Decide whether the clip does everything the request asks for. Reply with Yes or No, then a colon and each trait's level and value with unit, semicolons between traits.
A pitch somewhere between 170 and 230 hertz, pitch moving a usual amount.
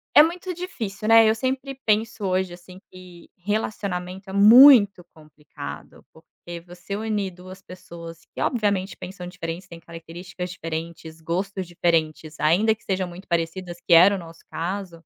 Yes: medium, 185 Hz; average, 3.4 semitones